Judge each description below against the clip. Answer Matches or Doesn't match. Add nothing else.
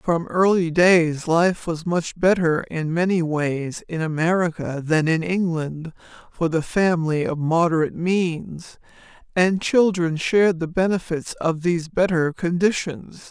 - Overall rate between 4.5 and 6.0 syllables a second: Doesn't match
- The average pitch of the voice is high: Doesn't match